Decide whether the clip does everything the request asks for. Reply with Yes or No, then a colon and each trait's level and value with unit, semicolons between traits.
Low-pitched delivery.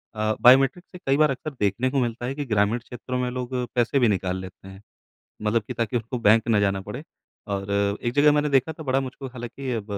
Yes: low, 120 Hz